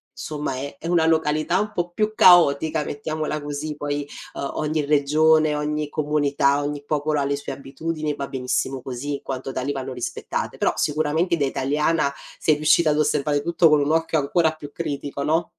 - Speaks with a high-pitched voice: No, medium, 150 Hz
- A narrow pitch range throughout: Yes, narrow, 1.8 semitones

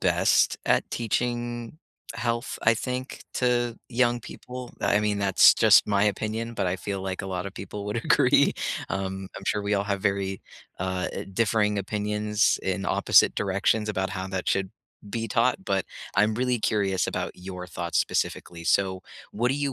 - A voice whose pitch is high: No, low, 105 Hz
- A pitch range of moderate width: Yes, average, 3.4 semitones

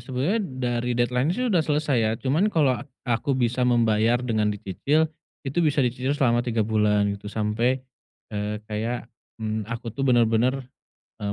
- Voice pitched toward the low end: Yes, low, 120 Hz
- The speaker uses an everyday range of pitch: Yes, average, 3.5 semitones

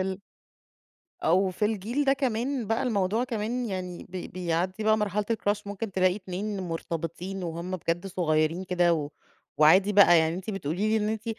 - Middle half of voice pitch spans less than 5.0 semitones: Yes, average, 3.5 semitones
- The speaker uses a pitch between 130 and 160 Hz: No, high, 190 Hz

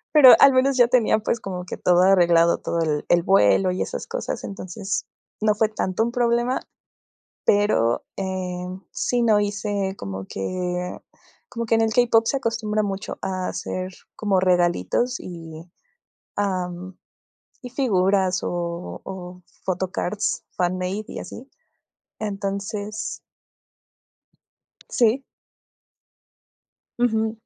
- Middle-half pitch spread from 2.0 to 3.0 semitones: No, average, 3.7 semitones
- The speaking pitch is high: Yes, high, 195 Hz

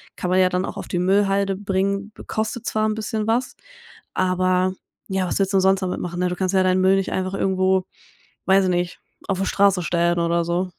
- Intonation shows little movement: Yes, narrow, 1.3 semitones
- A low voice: No, high, 190 Hz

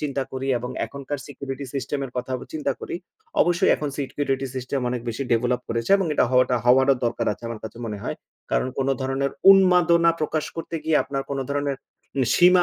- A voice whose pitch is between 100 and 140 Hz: Yes, low, 135 Hz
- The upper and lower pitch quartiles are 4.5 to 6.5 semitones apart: No, average, 2.9 semitones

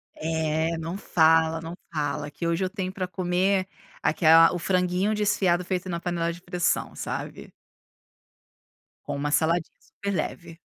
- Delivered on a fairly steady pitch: Yes, narrow, 2.2 semitones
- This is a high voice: No, medium, 175 Hz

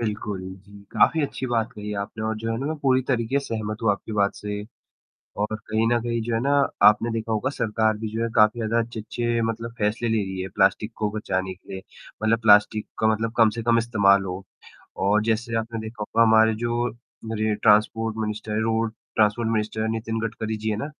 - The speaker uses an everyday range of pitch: No, narrow, 1.5 semitones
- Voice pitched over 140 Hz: No, low, 110 Hz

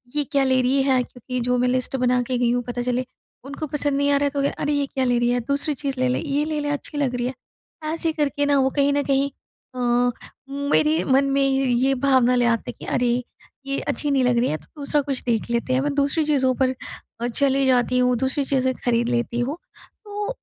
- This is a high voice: Yes, very high, 265 Hz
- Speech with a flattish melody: Yes, narrow, 2.3 semitones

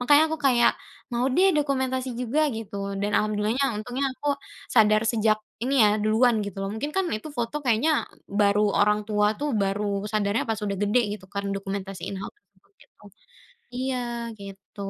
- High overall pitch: Yes, high, 220 Hz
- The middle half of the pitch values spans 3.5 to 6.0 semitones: Yes, average, 4.1 semitones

